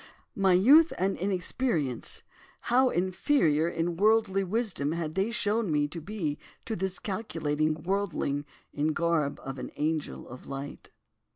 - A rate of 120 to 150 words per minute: Yes, average, 145 wpm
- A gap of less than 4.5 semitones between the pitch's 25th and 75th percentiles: No, average, 5.2 semitones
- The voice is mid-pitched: Yes, medium, 175 Hz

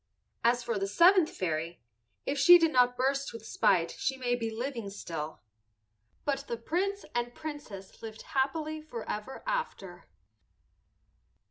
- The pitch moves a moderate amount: No, wide, 5.9 semitones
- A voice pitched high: Yes, high, 245 Hz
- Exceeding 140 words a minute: No, slow, 135 wpm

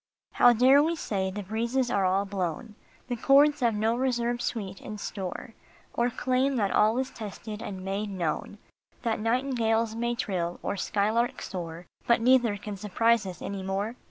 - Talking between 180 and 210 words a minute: No, average, 170 wpm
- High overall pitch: Yes, high, 220 Hz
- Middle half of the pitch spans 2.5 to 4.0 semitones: Yes, average, 3.5 semitones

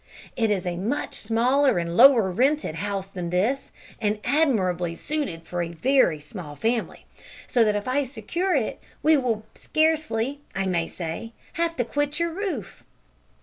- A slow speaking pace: No, average, 160 wpm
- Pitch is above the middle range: Yes, high, 225 Hz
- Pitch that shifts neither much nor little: No, wide, 7.7 semitones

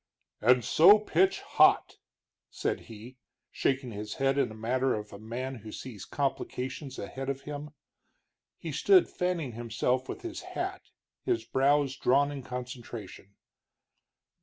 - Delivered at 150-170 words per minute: No, slow, 135 wpm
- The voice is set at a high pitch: No, low, 130 Hz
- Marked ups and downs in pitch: No, average, 3.6 semitones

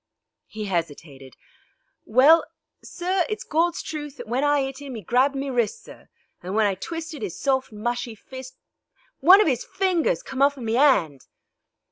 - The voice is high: Yes, very high, 265 Hz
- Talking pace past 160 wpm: Yes, average, 170 wpm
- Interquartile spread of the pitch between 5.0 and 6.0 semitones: Yes, wide, 5.6 semitones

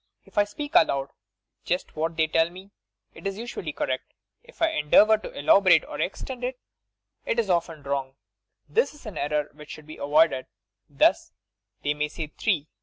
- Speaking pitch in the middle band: Yes, medium, 165 Hz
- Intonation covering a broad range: Yes, wide, 5.9 semitones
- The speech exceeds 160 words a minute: Yes, average, 180 wpm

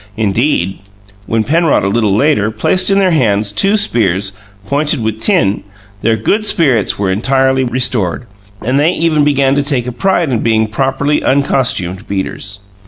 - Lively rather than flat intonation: Yes, wide, 5.7 semitones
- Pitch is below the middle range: Yes, low, 125 Hz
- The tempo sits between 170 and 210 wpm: No, average, 160 wpm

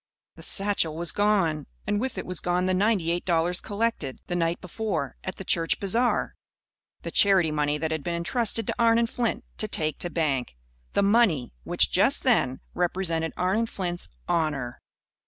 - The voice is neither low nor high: Yes, medium, 175 Hz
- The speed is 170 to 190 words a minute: Yes, average, 175 wpm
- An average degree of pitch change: Yes, average, 4.2 semitones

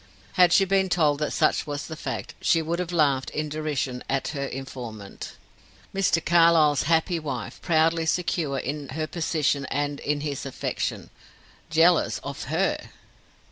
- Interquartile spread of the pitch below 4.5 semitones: Yes, average, 3.0 semitones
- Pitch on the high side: No, medium, 155 Hz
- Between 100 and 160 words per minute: Yes, average, 150 wpm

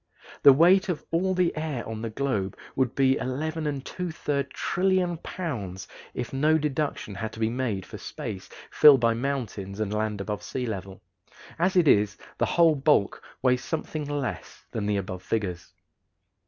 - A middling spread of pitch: No, wide, 6.7 semitones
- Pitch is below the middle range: Yes, low, 130 Hz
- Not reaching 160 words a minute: No, average, 165 wpm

